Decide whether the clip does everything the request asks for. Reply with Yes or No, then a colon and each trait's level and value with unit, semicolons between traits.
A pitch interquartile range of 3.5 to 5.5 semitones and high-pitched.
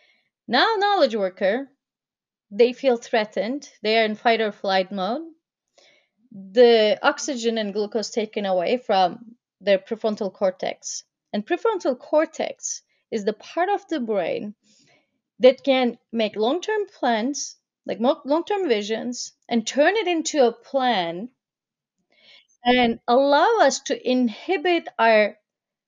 Yes: average, 4.6 semitones; high, 240 Hz